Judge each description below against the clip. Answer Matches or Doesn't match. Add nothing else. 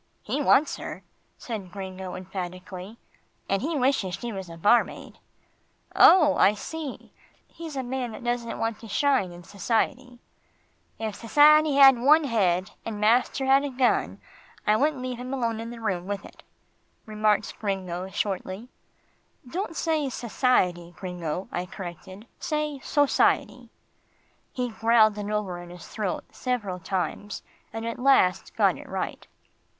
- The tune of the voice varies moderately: Doesn't match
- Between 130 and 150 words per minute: Matches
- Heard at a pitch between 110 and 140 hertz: Doesn't match